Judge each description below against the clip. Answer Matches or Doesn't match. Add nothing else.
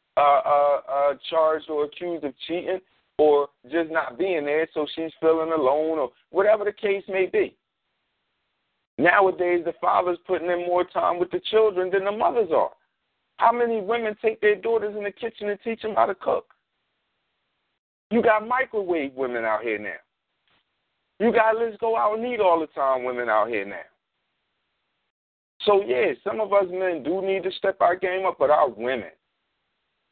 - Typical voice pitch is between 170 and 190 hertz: Matches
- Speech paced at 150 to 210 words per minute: Matches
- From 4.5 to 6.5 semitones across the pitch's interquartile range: Matches